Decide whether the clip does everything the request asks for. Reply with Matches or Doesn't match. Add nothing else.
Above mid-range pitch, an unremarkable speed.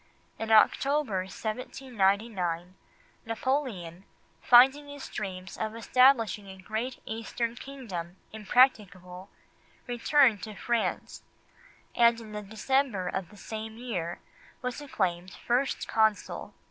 Doesn't match